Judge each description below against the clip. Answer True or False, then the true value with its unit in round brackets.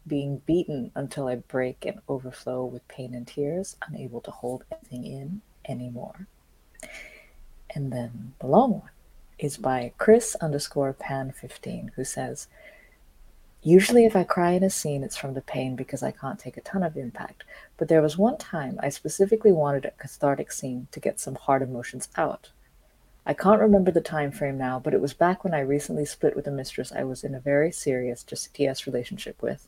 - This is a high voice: False (140 Hz)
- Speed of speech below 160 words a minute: False (190 wpm)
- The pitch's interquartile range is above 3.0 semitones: True (5.2 semitones)